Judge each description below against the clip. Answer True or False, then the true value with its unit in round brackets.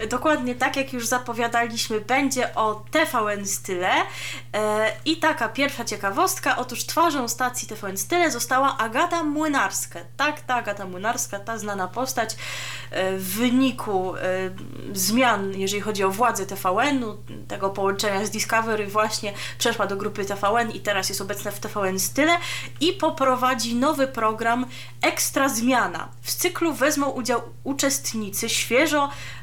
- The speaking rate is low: False (130 wpm)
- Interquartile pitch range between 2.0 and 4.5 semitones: False (4.9 semitones)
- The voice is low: False (230 Hz)